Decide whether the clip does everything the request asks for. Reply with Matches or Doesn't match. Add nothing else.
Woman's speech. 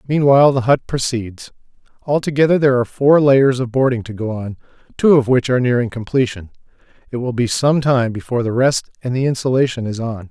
Doesn't match